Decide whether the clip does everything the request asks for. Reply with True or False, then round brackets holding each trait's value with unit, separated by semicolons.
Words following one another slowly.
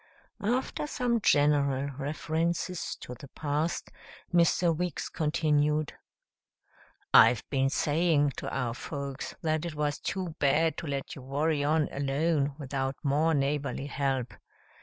True (125 wpm)